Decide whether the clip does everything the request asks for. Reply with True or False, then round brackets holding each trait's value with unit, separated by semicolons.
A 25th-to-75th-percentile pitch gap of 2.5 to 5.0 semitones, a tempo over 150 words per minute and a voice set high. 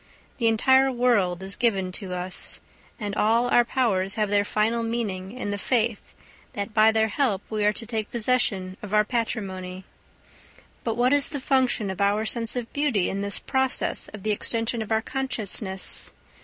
True (3.2 semitones; 180 wpm; 220 Hz)